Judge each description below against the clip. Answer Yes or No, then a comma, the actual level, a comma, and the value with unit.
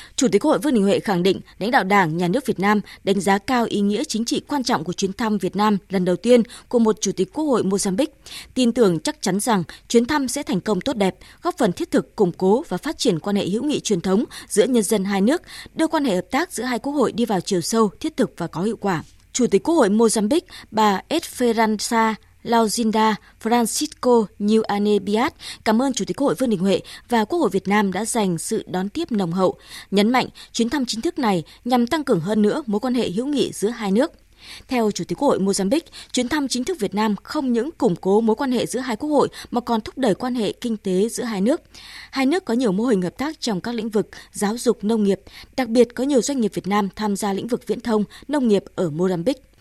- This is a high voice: Yes, high, 220 Hz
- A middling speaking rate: No, fast, 255 wpm